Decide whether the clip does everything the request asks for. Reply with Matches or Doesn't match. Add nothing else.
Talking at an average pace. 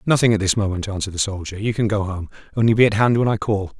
Doesn't match